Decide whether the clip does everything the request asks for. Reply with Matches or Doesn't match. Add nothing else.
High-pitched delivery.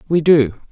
Doesn't match